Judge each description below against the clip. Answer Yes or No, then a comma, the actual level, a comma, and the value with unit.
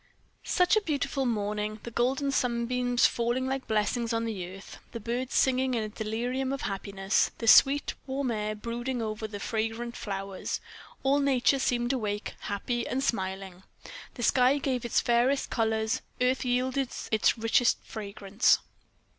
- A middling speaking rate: Yes, average, 150 wpm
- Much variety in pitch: No, average, 3.3 semitones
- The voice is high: Yes, high, 235 Hz